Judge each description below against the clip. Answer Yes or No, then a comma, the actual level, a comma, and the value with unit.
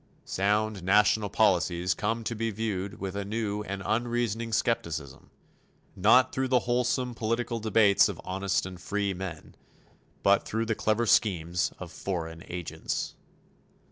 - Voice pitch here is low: Yes, low, 105 Hz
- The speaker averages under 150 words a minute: Yes, average, 140 wpm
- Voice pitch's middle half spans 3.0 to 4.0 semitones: Yes, average, 3.5 semitones